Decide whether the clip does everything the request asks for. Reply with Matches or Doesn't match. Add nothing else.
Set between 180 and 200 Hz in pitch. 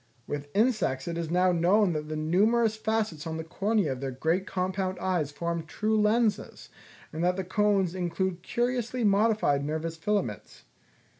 Matches